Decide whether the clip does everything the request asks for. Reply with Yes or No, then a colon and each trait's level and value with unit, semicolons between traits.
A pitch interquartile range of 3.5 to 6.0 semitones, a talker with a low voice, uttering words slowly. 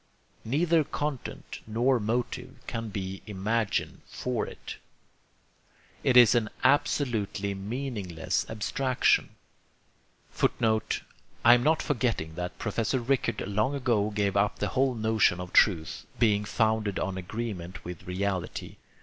Yes: average, 3.9 semitones; low, 110 Hz; slow, 120 wpm